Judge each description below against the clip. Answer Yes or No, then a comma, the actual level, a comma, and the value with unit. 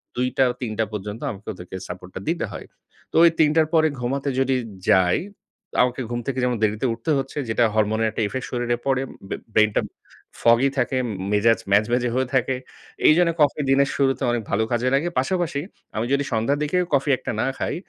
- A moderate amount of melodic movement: Yes, average, 3.9 semitones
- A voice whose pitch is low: Yes, low, 125 Hz